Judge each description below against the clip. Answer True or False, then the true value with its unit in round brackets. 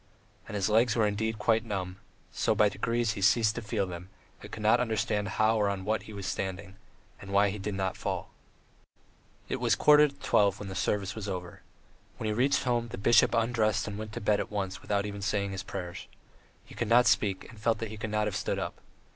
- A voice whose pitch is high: False (105 Hz)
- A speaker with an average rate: False (235 wpm)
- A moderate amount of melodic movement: False (2.1 semitones)